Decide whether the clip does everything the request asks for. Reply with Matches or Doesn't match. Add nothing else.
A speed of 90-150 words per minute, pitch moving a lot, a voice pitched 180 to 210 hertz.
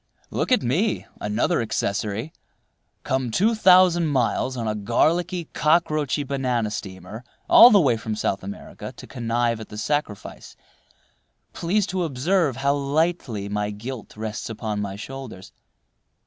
Doesn't match